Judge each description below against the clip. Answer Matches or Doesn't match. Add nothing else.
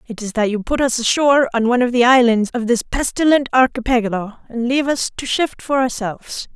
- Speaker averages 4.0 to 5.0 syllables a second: Doesn't match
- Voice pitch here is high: Matches